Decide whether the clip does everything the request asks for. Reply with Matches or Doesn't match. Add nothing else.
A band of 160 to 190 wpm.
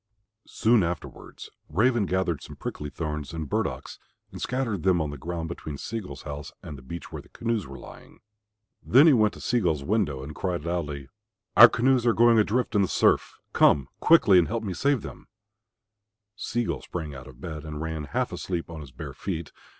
Doesn't match